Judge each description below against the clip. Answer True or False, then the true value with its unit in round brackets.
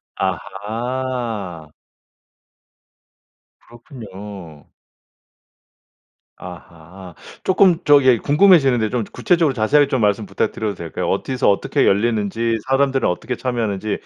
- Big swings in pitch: False (5.0 semitones)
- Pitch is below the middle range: True (115 Hz)